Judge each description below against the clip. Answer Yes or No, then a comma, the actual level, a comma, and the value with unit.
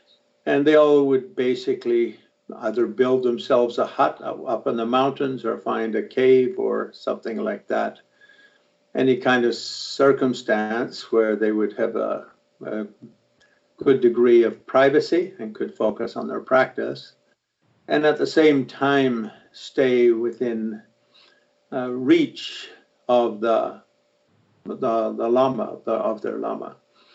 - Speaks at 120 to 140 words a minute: Yes, slow, 135 wpm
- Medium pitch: No, low, 130 Hz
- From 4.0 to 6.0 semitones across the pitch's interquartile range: Yes, average, 4.8 semitones